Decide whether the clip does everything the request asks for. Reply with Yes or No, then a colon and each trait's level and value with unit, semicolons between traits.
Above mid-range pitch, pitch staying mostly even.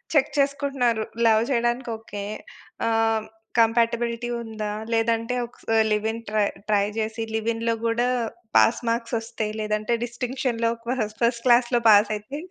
Yes: high, 230 Hz; narrow, 1.6 semitones